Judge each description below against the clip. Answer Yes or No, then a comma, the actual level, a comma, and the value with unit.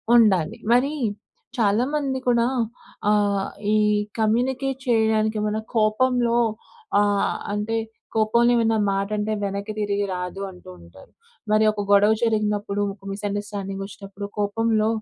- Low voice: No, high, 215 Hz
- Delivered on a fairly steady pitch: Yes, narrow, 2.2 semitones